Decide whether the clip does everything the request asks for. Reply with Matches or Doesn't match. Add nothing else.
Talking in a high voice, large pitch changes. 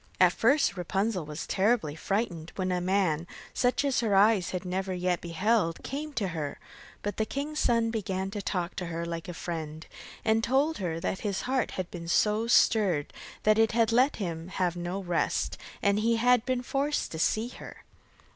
Doesn't match